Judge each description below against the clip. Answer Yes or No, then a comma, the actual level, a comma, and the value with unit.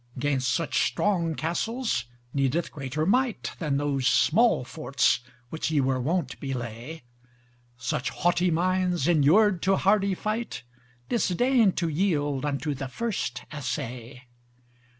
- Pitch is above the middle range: No, medium, 160 Hz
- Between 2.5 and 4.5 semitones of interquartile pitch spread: No, wide, 5.6 semitones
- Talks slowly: Yes, slow, 120 wpm